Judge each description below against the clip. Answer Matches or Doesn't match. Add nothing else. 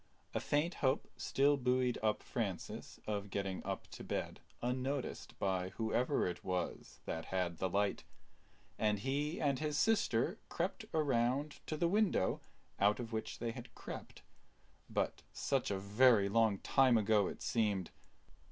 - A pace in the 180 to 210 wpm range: Doesn't match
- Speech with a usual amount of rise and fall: Doesn't match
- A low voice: Matches